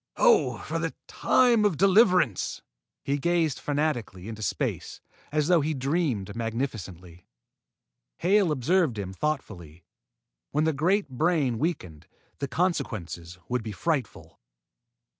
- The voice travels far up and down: Yes, wide, 7.9 semitones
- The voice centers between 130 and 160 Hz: Yes, medium, 140 Hz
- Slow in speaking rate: Yes, slow, 120 wpm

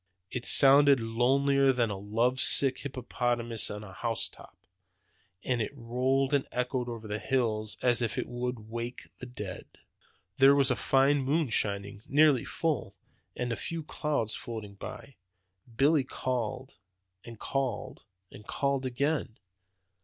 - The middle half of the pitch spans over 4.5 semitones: No, average, 3.3 semitones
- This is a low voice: Yes, low, 125 Hz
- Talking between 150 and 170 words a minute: No, average, 140 wpm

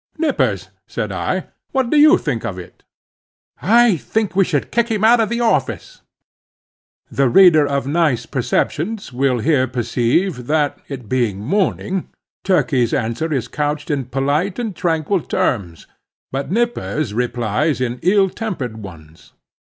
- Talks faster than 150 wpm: No, average, 145 wpm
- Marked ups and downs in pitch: Yes, wide, 8.0 semitones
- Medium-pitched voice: Yes, medium, 150 Hz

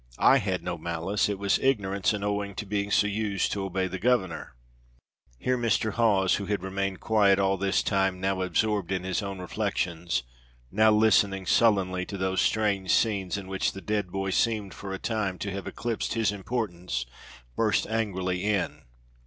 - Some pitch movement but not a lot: No, narrow, 2.1 semitones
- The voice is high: No, low, 100 Hz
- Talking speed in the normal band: Yes, average, 175 wpm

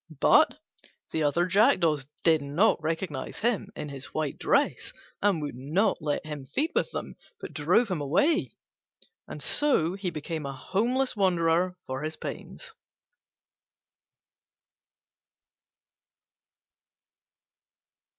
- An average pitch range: Yes, average, 4.8 semitones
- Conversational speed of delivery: No, slow, 110 wpm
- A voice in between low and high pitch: Yes, medium, 165 Hz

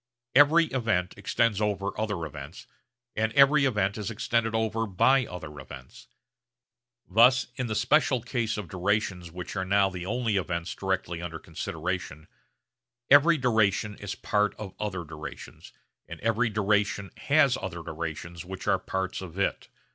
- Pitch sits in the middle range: No, low, 100 Hz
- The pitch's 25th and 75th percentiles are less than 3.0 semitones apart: No, average, 4.2 semitones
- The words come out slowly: No, average, 145 wpm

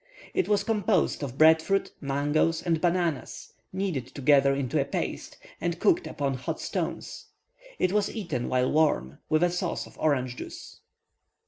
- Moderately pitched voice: Yes, medium, 155 Hz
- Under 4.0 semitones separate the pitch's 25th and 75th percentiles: No, average, 4.7 semitones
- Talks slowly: No, average, 155 wpm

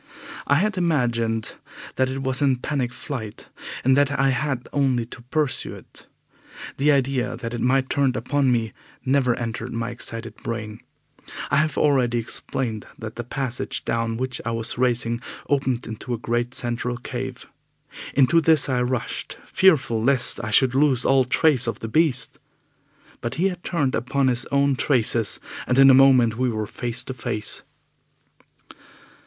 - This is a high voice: No, low, 125 Hz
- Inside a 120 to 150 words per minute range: No, average, 160 wpm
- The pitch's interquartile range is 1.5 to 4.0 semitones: Yes, average, 2.8 semitones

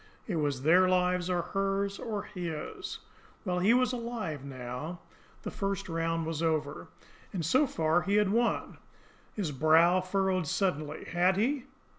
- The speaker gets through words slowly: No, average, 150 wpm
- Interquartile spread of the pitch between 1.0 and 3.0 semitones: No, average, 3.7 semitones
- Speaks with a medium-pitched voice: Yes, medium, 180 Hz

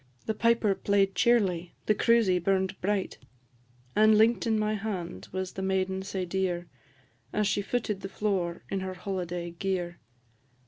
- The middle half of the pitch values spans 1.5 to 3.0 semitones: Yes, narrow, 2.5 semitones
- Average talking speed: Yes, average, 150 wpm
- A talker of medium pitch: No, high, 195 Hz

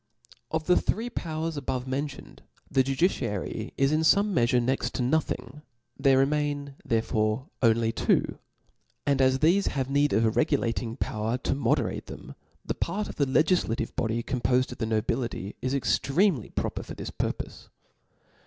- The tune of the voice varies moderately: Yes, average, 4.2 semitones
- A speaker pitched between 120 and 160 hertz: Yes, low, 135 Hz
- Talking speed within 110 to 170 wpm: Yes, average, 160 wpm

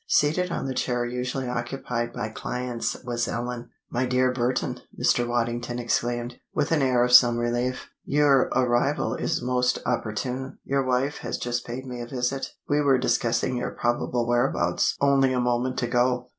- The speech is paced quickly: No, average, 165 wpm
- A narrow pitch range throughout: Yes, narrow, 1.3 semitones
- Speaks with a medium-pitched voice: No, low, 125 Hz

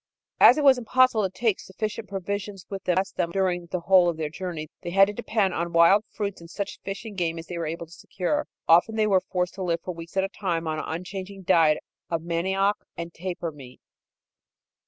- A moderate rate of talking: No, fast, 230 wpm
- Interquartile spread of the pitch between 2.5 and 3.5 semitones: Yes, average, 2.9 semitones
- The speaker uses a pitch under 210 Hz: Yes, medium, 185 Hz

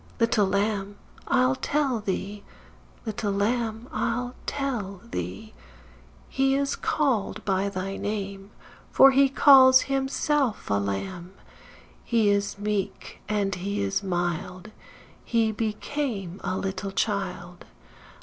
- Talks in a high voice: Yes, high, 205 Hz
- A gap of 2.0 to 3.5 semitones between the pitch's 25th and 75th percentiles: No, average, 4.3 semitones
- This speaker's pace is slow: Yes, slow, 110 wpm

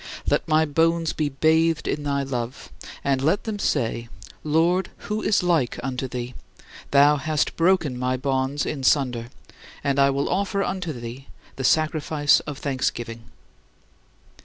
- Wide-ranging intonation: No, average, 3.6 semitones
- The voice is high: No, medium, 145 Hz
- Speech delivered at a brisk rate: No, average, 140 wpm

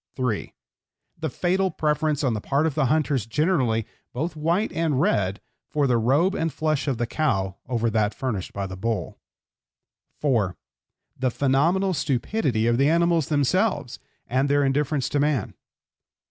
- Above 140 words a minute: Yes, average, 150 wpm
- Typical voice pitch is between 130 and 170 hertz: Yes, medium, 140 Hz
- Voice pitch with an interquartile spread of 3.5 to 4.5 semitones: No, average, 5.0 semitones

